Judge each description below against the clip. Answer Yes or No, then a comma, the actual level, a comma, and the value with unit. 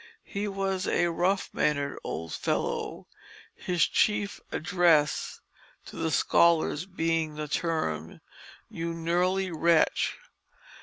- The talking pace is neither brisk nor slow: No, slow, 105 wpm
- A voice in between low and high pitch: Yes, medium, 170 Hz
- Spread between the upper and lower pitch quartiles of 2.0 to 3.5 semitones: Yes, average, 3.0 semitones